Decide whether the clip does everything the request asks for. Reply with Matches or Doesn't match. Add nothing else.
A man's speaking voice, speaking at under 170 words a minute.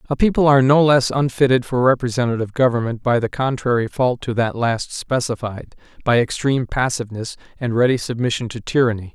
Matches